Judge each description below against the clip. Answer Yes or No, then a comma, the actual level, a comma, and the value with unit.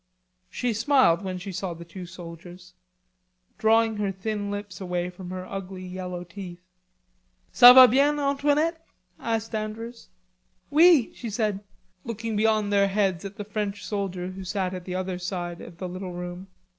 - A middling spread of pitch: Yes, average, 3.5 semitones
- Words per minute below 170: Yes, average, 160 wpm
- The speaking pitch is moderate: No, high, 195 Hz